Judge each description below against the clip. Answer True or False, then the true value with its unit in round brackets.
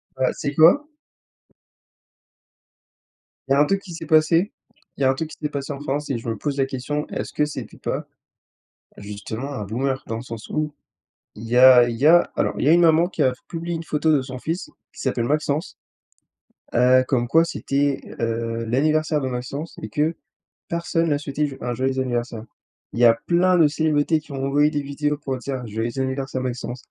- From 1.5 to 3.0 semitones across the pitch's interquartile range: False (3.7 semitones)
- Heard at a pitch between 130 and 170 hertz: True (140 Hz)